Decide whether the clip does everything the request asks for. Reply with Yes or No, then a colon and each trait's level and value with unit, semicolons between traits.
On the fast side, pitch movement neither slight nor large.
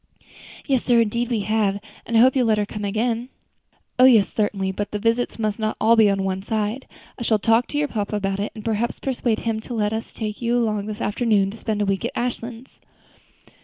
No: fast, 235 wpm; narrow, 2.3 semitones